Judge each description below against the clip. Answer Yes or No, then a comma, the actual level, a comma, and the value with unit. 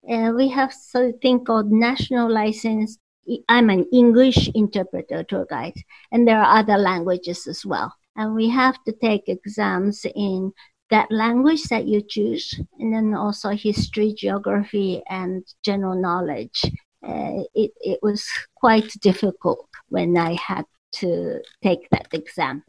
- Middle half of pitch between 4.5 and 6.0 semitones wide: No, average, 3.2 semitones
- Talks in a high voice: Yes, high, 215 Hz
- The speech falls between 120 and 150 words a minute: Yes, average, 140 wpm